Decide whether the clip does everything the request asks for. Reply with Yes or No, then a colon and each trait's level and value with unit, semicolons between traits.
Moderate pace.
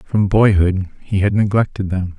Yes: average, 165 wpm